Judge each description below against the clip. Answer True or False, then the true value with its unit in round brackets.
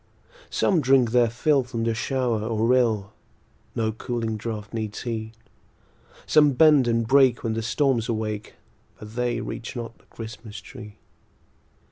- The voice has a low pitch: True (115 Hz)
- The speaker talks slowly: False (145 wpm)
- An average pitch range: False (2.3 semitones)